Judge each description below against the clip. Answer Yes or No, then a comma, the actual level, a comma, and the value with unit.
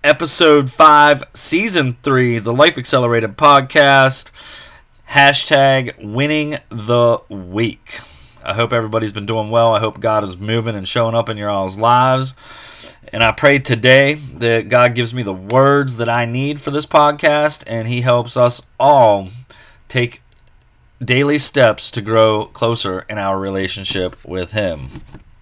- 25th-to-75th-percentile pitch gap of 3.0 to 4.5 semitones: Yes, average, 3.8 semitones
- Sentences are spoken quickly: No, average, 145 wpm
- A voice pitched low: Yes, low, 120 Hz